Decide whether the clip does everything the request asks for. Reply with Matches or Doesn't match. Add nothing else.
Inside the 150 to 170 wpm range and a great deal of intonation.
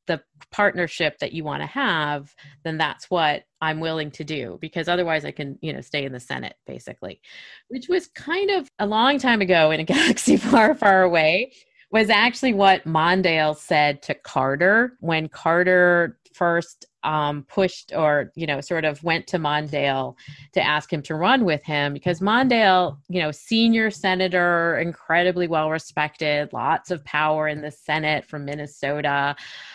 Doesn't match